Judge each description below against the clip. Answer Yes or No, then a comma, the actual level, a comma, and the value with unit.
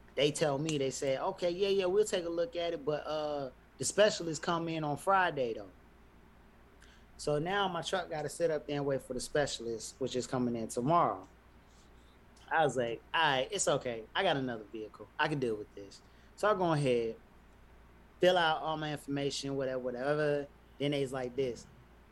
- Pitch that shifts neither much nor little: Yes, average, 4.8 semitones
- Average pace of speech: Yes, average, 195 wpm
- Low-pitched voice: No, medium, 145 Hz